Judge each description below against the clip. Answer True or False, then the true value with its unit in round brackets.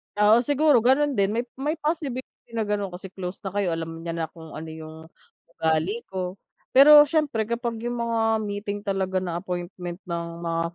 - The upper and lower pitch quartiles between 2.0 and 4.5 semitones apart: False (5.5 semitones)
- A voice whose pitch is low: False (200 Hz)